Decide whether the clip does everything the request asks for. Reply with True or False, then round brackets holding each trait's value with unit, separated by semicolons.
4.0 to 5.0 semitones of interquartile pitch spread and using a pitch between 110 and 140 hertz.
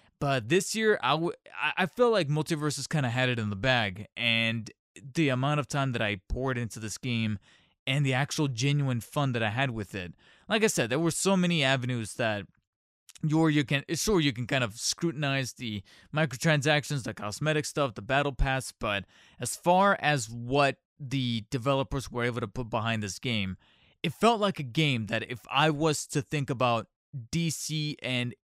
True (4.7 semitones; 135 Hz)